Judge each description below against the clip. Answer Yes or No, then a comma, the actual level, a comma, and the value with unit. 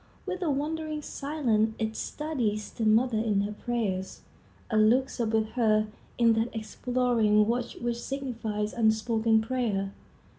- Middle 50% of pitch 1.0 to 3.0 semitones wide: Yes, narrow, 2.6 semitones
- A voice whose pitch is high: Yes, high, 225 Hz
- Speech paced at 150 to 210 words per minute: No, average, 140 wpm